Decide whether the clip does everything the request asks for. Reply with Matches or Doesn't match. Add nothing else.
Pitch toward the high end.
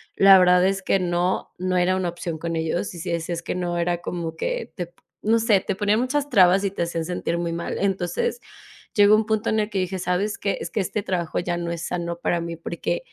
Doesn't match